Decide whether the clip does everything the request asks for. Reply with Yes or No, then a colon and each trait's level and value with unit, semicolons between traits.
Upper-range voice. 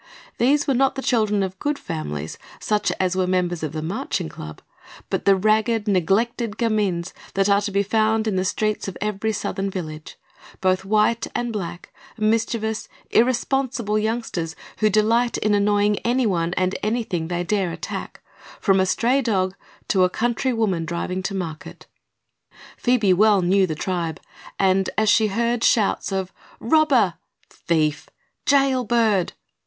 Yes: high, 205 Hz